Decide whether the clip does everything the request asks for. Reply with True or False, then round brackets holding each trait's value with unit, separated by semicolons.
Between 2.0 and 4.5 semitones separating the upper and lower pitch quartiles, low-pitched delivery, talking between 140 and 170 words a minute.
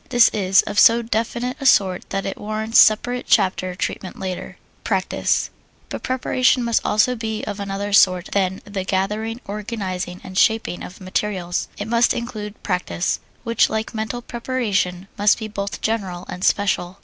False (3.3 semitones; 205 Hz; 160 wpm)